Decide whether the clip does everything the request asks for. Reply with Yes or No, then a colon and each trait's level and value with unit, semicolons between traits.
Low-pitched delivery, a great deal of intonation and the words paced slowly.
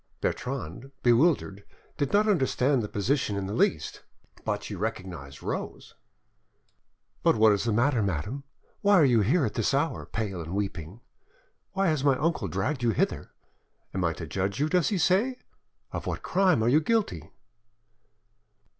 No: low, 120 Hz; wide, 7.6 semitones; average, 165 wpm